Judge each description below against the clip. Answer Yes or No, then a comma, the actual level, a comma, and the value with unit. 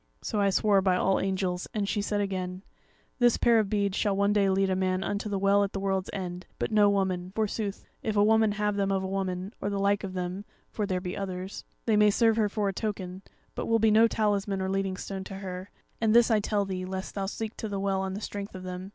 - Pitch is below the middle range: No, high, 195 Hz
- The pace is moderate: No, fast, 255 wpm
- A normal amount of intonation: No, narrow, 1.6 semitones